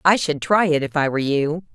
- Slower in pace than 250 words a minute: No, fast, 275 wpm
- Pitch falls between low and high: Yes, medium, 160 Hz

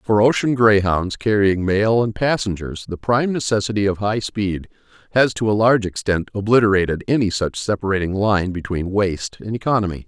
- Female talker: No, male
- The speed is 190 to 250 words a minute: No, average, 160 wpm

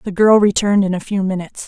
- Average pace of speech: No, fast, 250 wpm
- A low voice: No, high, 200 Hz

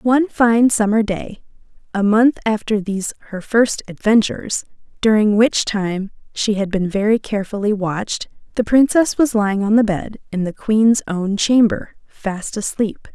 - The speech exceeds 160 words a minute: No, average, 155 wpm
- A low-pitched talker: No, high, 215 Hz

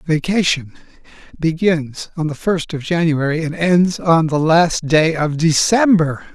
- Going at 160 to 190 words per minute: No, average, 140 wpm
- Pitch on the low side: No, medium, 160 Hz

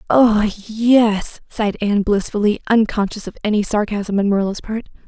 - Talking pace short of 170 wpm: Yes, average, 140 wpm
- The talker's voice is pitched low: No, high, 210 Hz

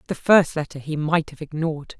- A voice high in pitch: No, medium, 155 Hz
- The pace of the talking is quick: Yes, fast, 210 wpm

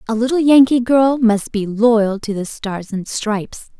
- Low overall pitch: No, high, 225 Hz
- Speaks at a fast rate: No, average, 190 wpm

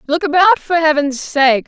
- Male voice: No, female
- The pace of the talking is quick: No, average, 180 wpm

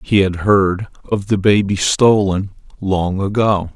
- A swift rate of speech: No, average, 145 wpm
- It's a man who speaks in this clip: Yes, male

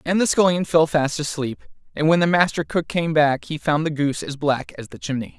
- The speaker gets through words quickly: Yes, fast, 245 wpm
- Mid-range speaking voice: Yes, medium, 155 Hz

